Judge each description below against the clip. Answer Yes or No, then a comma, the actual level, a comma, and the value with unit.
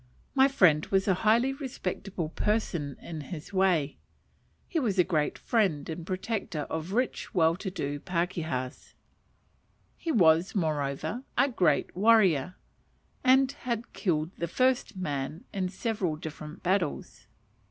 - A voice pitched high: No, medium, 180 Hz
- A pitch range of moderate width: No, wide, 5.8 semitones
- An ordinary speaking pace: No, slow, 130 wpm